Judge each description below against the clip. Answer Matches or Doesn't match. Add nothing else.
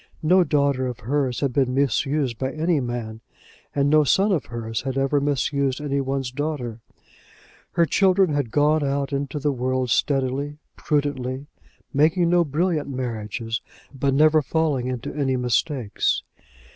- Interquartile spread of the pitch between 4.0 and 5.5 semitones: Doesn't match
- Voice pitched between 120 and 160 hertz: Matches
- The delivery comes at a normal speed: Matches